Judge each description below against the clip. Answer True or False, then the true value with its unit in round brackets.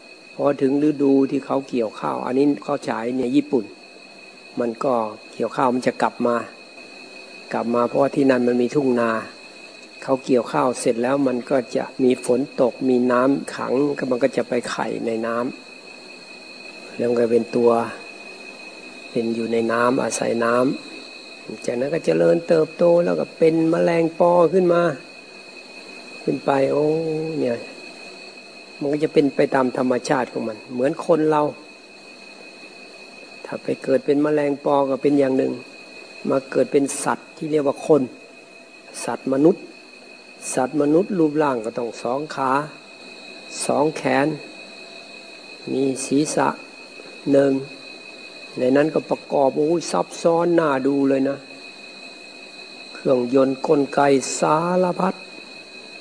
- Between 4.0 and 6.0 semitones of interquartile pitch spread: False (3.3 semitones)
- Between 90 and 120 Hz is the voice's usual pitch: False (135 Hz)